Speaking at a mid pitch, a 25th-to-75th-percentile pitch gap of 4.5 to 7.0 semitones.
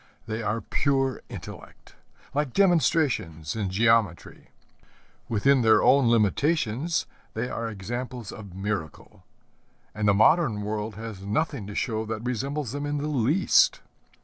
No: low, 115 Hz; average, 4.9 semitones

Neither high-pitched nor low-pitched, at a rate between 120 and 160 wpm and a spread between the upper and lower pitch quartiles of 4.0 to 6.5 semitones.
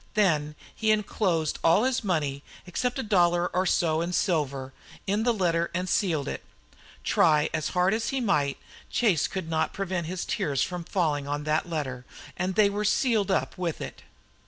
No: medium, 175 Hz; average, 180 wpm; average, 4.5 semitones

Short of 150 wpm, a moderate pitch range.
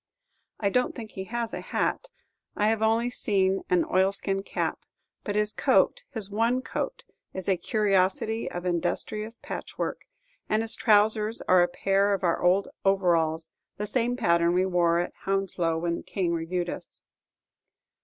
No: average, 160 wpm; average, 3.6 semitones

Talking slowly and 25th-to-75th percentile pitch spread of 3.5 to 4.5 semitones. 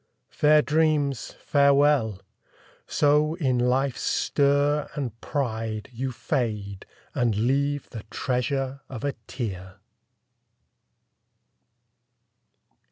Yes: slow, 85 wpm; average, 3.8 semitones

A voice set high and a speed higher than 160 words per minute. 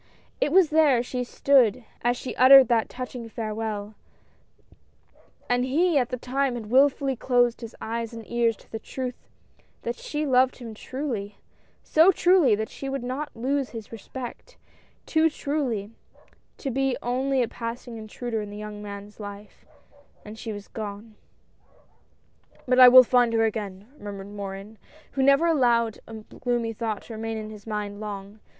Yes: high, 235 Hz; average, 170 wpm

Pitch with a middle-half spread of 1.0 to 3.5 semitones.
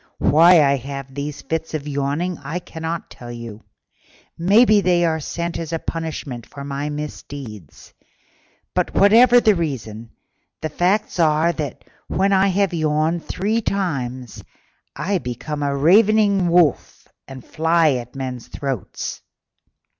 No: average, 4.3 semitones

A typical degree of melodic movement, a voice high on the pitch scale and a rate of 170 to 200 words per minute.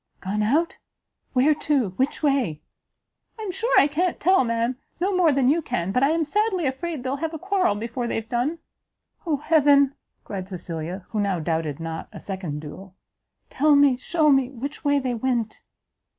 No: wide, 6.9 semitones; very high, 265 Hz; average, 180 wpm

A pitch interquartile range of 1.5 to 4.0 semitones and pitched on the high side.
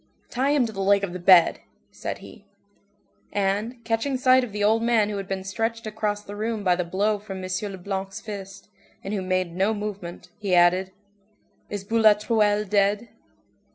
Yes: narrow, 2.4 semitones; high, 205 Hz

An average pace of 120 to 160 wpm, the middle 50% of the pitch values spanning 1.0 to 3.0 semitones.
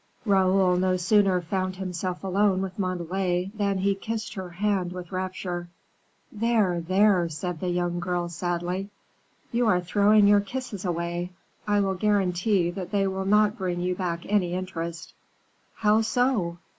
Yes: average, 150 wpm; narrow, 2.4 semitones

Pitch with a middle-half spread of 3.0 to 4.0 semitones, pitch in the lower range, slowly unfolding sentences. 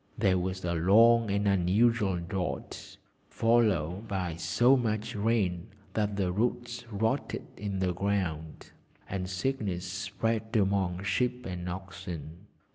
Yes: average, 3.7 semitones; low, 100 Hz; slow, 120 wpm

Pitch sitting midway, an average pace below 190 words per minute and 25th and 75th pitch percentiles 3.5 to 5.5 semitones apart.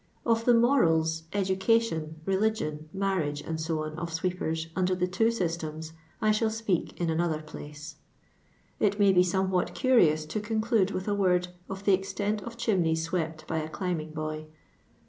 Yes: medium, 180 Hz; average, 155 wpm; average, 4.2 semitones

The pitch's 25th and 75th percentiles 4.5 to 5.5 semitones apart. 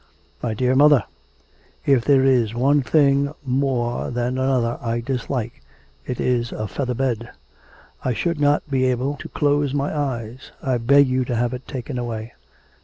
No: average, 2.7 semitones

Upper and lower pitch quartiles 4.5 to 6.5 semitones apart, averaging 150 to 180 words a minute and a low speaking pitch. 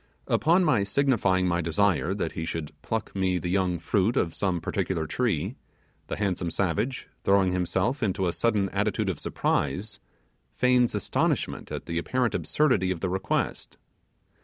No: average, 3.5 semitones; average, 155 wpm; very low, 95 Hz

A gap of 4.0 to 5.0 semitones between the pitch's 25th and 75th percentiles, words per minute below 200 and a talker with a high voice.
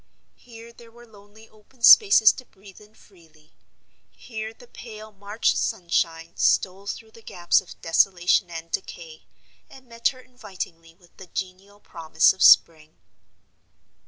Yes: average, 4.6 semitones; average, 140 wpm; high, 200 Hz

